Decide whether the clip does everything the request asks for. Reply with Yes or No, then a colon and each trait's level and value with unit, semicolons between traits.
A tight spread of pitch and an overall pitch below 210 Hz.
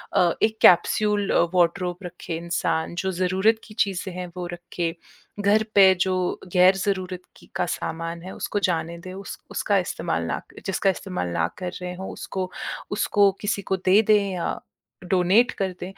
Yes: narrow, 2.0 semitones; medium, 185 Hz